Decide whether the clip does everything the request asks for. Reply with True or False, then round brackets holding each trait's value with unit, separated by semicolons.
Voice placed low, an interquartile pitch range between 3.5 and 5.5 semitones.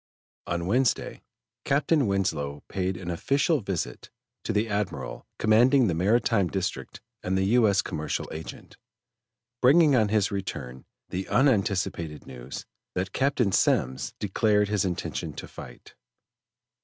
True (100 Hz; 4.7 semitones)